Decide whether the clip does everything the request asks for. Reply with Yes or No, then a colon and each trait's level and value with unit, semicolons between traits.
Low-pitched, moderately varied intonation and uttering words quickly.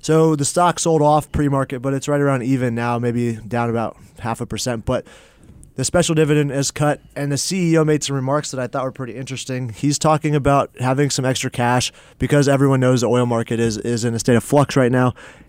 Yes: low, 130 Hz; average, 3.3 semitones; fast, 225 wpm